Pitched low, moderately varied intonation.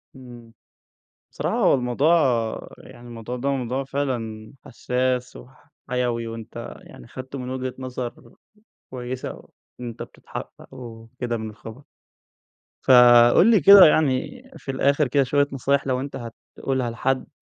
No: low, 125 Hz; narrow, 2.1 semitones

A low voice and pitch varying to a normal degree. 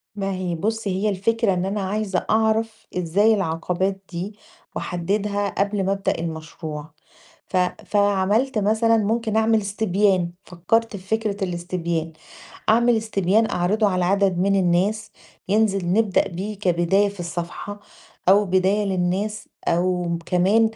No: high, 195 Hz; average, 3.1 semitones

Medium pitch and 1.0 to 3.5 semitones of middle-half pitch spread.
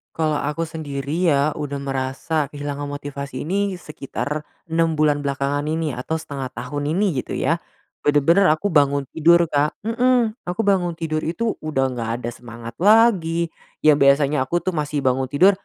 Yes: medium, 150 Hz; average, 3.2 semitones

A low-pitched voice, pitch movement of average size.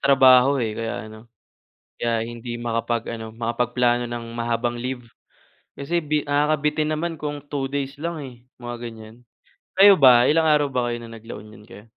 Yes: low, 120 Hz; average, 3.5 semitones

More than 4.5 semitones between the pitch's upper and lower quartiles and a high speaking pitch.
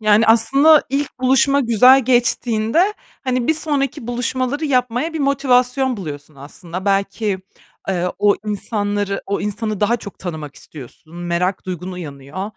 Yes: wide, 5.6 semitones; high, 220 Hz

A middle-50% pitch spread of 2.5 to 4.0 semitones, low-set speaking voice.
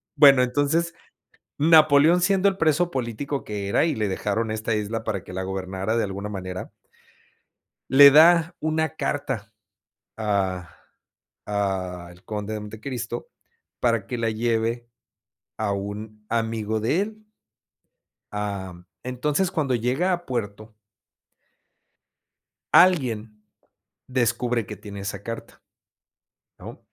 No: wide, 5.6 semitones; low, 115 Hz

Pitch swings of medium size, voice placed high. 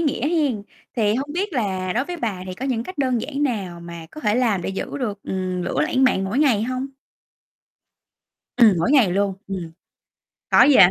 No: wide, 6.0 semitones; high, 225 Hz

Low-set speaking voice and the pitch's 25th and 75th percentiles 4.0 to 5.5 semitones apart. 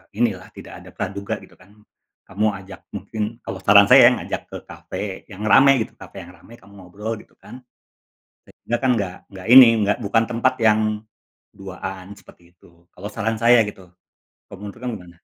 No: low, 105 Hz; average, 3.0 semitones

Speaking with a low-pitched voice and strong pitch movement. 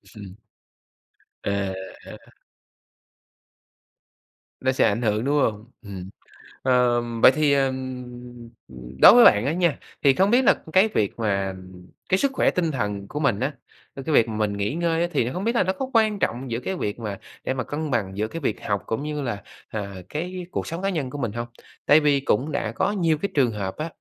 Yes: low, 130 Hz; wide, 7.5 semitones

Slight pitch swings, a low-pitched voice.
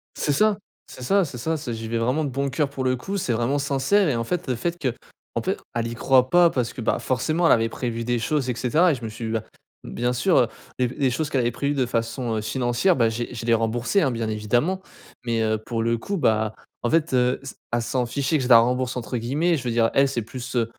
No: average, 3.4 semitones; low, 125 Hz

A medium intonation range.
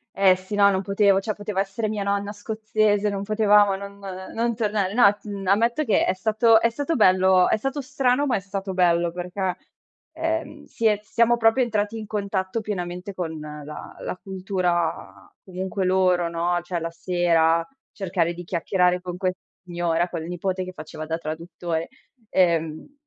Yes: average, 3.3 semitones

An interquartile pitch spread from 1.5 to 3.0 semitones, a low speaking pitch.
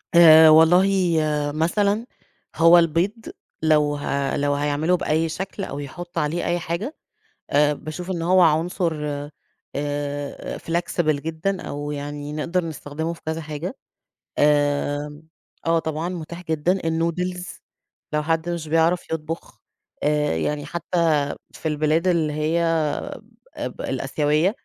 No: narrow, 2.5 semitones; medium, 160 Hz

